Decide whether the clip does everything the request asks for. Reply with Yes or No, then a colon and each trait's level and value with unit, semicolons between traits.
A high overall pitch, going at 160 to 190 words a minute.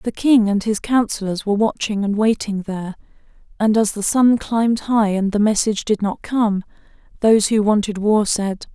Yes: high, 210 Hz; average, 185 wpm